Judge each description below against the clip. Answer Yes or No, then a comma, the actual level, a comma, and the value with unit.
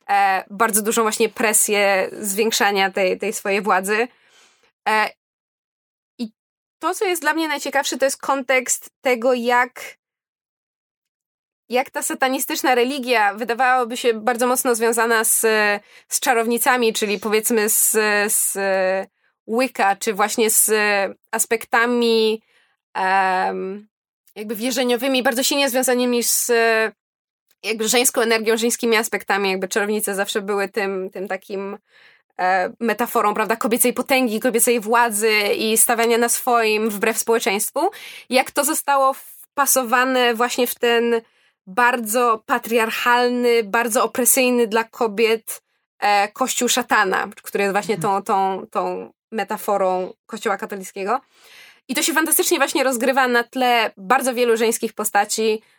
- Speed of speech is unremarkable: Yes, average, 120 wpm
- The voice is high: Yes, high, 230 Hz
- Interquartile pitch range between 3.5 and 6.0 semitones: No, average, 3.0 semitones